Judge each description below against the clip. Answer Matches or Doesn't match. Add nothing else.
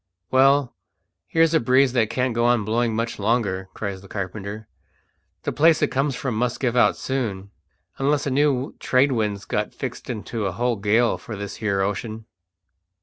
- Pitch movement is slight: Doesn't match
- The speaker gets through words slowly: Doesn't match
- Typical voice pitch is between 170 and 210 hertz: Doesn't match